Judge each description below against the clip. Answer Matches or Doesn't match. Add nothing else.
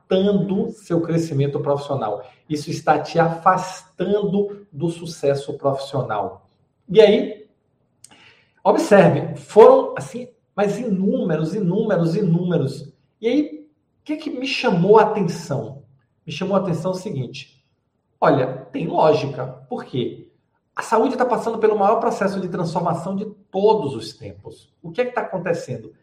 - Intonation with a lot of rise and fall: Matches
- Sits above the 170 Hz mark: Matches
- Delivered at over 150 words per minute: Doesn't match